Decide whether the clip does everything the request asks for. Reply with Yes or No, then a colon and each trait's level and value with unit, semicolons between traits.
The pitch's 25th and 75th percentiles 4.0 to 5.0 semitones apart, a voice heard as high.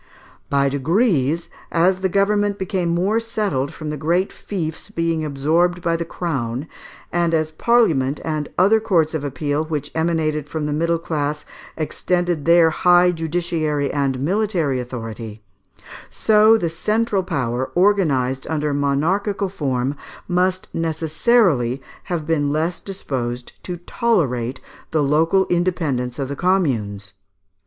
No: average, 4.3 semitones; medium, 160 Hz